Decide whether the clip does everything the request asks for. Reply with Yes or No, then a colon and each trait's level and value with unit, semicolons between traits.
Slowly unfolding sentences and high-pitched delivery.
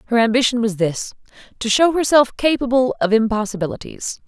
Yes: slow, 125 wpm; high, 235 Hz